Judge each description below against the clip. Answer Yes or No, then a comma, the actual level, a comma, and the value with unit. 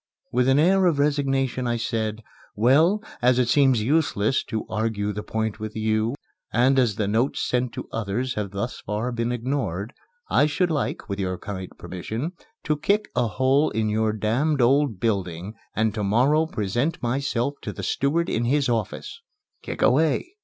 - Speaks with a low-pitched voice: Yes, low, 120 Hz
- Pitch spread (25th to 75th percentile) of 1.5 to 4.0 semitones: No, average, 4.4 semitones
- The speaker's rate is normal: Yes, average, 175 wpm